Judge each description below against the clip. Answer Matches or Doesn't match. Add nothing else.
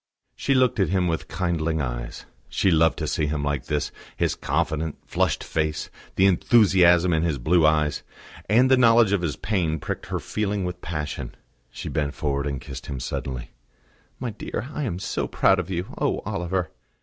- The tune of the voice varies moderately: Matches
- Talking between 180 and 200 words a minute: Matches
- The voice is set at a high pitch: Doesn't match